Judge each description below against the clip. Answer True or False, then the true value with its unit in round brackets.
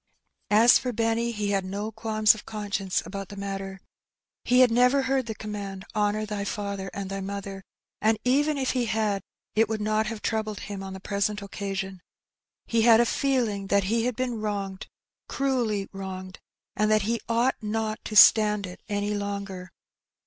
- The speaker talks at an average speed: True (180 wpm)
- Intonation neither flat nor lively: False (2.3 semitones)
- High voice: True (210 Hz)